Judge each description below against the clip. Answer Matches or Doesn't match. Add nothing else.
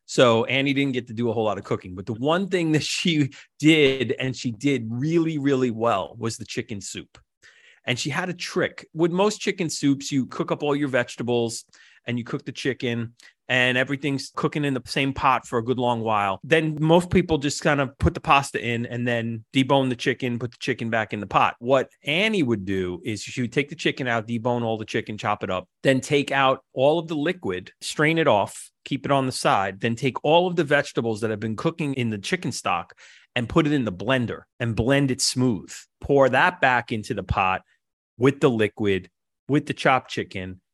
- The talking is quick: Matches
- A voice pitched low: Matches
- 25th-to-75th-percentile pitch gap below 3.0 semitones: Doesn't match